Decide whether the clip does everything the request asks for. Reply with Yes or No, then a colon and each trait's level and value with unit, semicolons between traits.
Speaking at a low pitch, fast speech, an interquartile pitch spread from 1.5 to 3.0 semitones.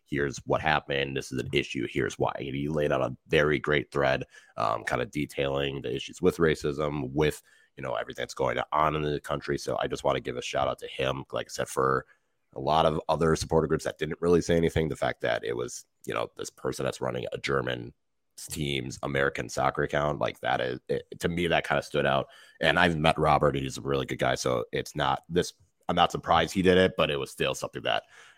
Yes: very low, 75 Hz; fast, 245 wpm; average, 2.7 semitones